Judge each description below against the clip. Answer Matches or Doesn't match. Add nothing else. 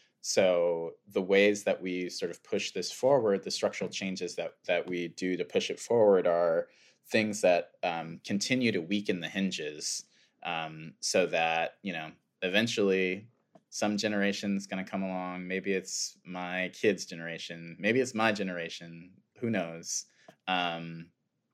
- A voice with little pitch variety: Doesn't match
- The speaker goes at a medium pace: Matches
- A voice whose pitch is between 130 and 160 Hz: Doesn't match